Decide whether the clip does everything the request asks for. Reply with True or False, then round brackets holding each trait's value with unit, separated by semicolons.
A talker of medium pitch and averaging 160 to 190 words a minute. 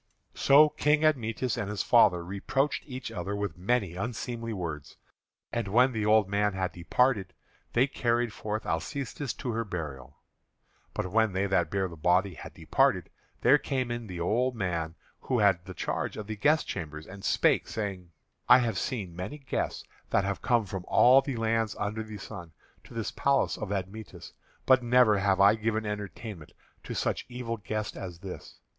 False (105 Hz; 175 wpm)